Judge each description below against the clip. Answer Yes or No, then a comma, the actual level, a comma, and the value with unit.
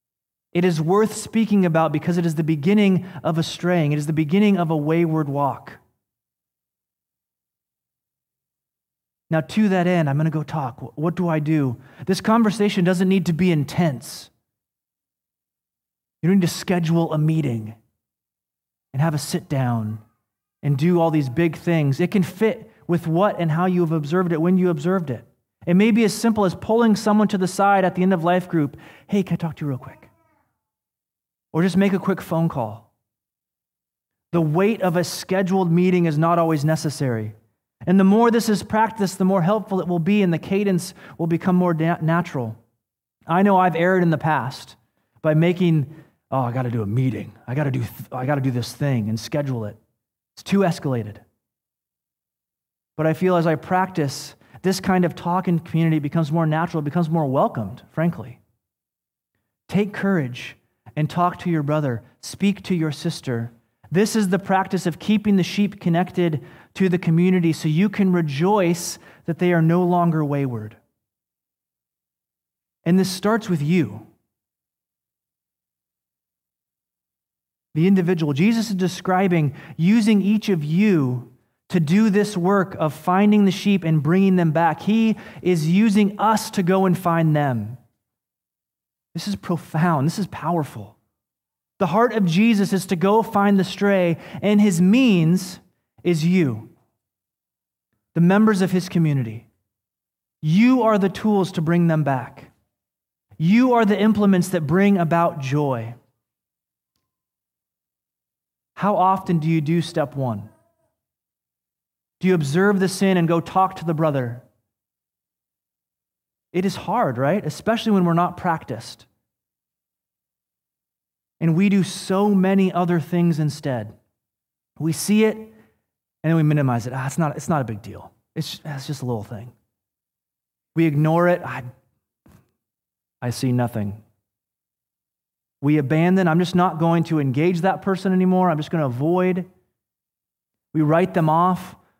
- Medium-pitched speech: Yes, medium, 165 Hz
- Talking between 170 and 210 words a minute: No, average, 160 wpm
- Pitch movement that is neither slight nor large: No, wide, 6.0 semitones